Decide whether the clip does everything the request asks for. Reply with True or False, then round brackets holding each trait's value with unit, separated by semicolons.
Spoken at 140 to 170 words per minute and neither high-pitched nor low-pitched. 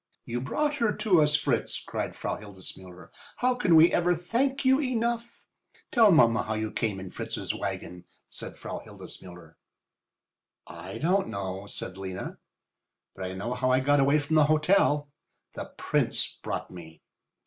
True (160 wpm; 145 Hz)